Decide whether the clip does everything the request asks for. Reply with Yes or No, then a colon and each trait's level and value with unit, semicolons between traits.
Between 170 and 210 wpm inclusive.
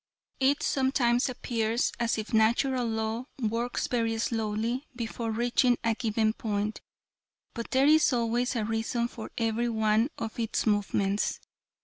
No: slow, 135 wpm